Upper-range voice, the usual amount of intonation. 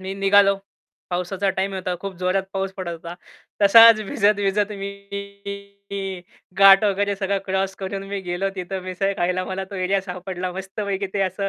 No: high, 195 Hz; narrow, 1.1 semitones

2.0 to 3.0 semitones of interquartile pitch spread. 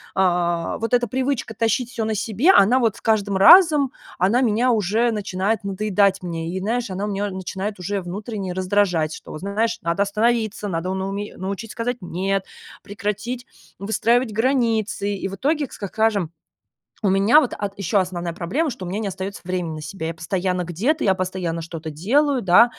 No: average, 3.6 semitones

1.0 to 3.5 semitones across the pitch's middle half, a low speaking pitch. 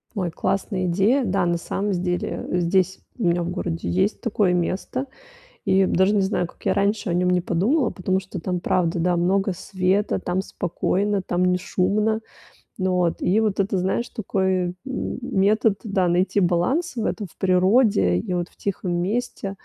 No: narrow, 2.4 semitones; high, 190 Hz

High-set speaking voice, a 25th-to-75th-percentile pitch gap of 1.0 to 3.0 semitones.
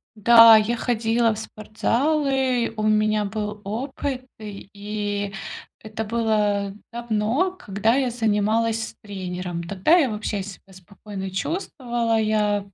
Yes: high, 215 Hz; narrow, 2.4 semitones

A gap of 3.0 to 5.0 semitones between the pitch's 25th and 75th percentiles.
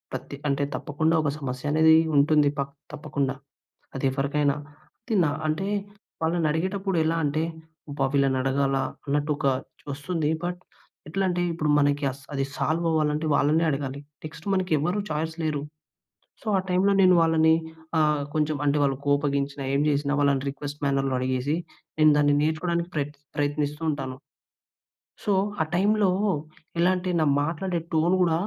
No: narrow, 2.5 semitones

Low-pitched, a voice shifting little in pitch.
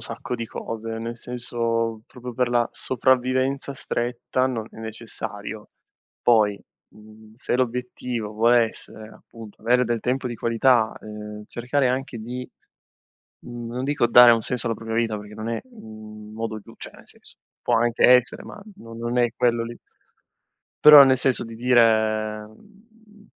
Yes: low, 120 Hz; narrow, 2.1 semitones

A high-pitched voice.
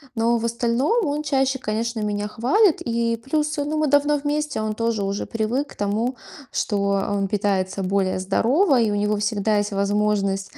Yes: high, 225 Hz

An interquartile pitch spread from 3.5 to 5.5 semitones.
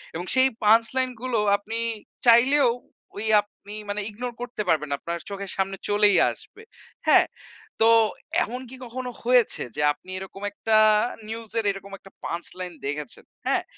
Yes: average, 3.9 semitones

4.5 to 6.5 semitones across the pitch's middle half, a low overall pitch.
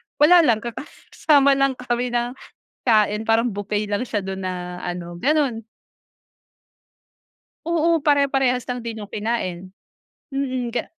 No: average, 4.8 semitones; high, 240 Hz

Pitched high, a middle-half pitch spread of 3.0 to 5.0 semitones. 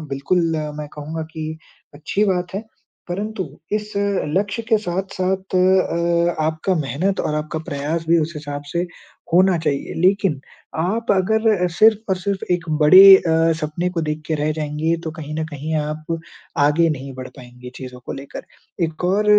No: medium, 165 Hz; average, 3.7 semitones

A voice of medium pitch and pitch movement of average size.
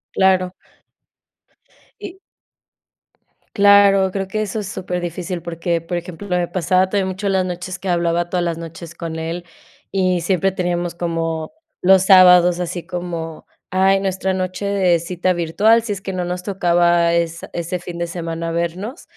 No: medium, 180 Hz; narrow, 1.9 semitones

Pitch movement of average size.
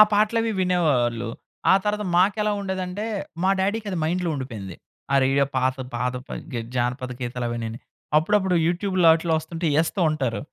No: wide, 7.1 semitones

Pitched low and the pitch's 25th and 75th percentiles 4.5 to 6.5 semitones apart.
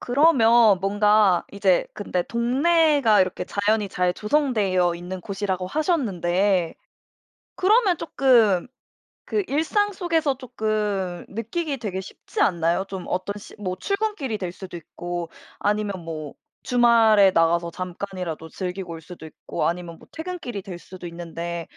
No: high, 200 Hz; wide, 5.5 semitones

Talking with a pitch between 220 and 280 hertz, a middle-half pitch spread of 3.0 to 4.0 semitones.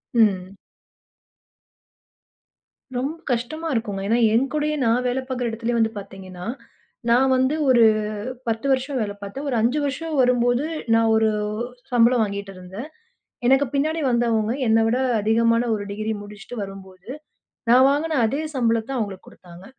Yes: high, 230 Hz; average, 3.7 semitones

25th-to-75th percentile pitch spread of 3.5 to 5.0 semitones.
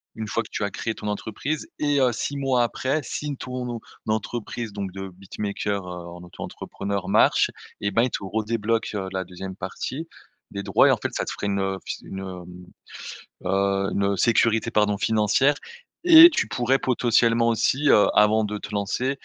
Yes: average, 3.8 semitones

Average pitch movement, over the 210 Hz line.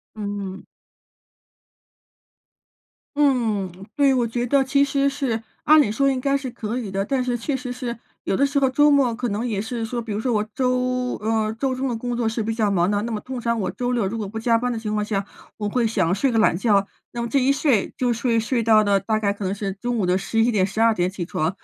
Yes: average, 3.3 semitones; high, 230 Hz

